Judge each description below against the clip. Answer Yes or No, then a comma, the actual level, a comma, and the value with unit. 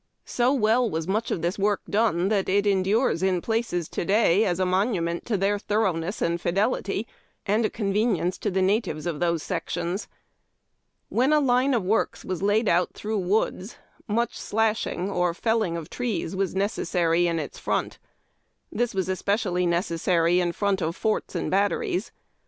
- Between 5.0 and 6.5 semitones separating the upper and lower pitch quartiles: No, average, 3.7 semitones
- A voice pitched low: No, high, 195 Hz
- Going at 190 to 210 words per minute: No, average, 170 wpm